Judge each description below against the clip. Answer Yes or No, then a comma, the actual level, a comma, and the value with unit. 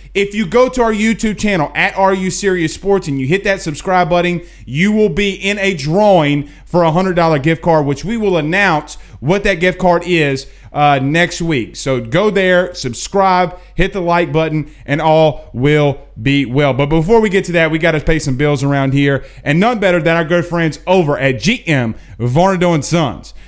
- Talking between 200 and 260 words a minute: Yes, fast, 205 wpm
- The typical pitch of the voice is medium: Yes, medium, 170 Hz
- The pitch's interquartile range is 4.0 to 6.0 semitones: Yes, average, 4.7 semitones